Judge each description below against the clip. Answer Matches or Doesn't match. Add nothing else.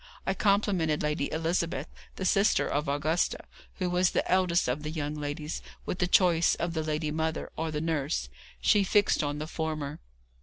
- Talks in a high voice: Doesn't match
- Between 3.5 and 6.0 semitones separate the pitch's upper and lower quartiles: Doesn't match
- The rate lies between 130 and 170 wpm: Doesn't match